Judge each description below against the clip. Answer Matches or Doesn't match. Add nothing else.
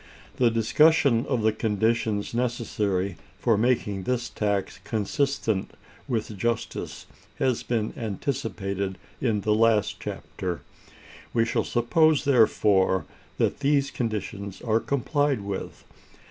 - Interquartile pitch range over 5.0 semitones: Doesn't match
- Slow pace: Matches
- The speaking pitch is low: Matches